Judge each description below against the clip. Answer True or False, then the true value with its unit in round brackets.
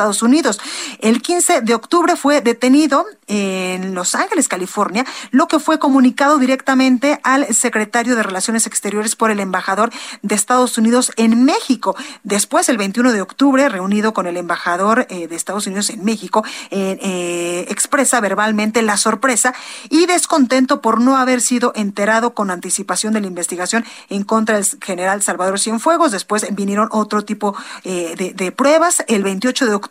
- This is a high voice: True (225 Hz)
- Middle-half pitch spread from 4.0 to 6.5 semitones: True (4.7 semitones)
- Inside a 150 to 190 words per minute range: True (165 wpm)